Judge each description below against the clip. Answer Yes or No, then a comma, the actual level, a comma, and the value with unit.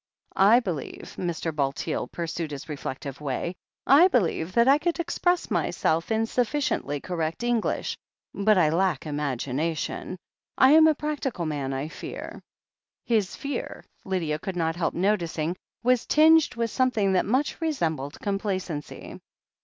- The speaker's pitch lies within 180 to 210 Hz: Yes, medium, 185 Hz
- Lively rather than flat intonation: Yes, wide, 7.9 semitones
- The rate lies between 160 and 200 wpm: No, average, 140 wpm